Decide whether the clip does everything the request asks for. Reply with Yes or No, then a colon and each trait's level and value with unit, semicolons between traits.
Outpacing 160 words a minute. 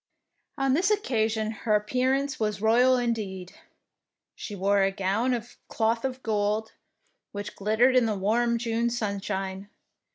No: slow, 135 wpm